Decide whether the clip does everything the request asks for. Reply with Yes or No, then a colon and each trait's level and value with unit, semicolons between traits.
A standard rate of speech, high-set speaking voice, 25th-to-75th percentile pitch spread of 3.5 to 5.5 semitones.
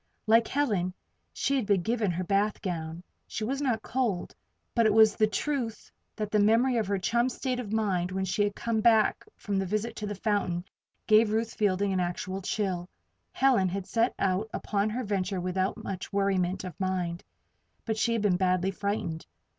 No: average, 185 wpm; high, 205 Hz; average, 3.1 semitones